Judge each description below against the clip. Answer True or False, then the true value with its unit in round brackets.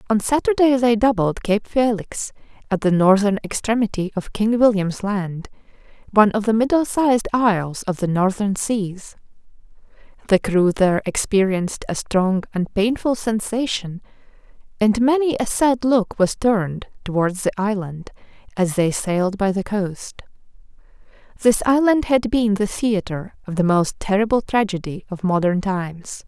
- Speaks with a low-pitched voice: False (205 Hz)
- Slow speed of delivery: False (145 wpm)